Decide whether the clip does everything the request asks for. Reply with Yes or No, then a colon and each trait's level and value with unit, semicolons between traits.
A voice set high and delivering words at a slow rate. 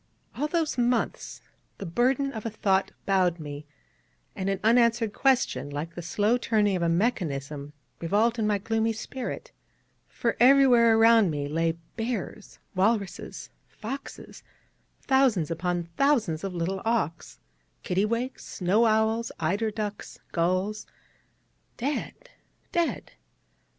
Yes: high, 215 Hz; slow, 120 wpm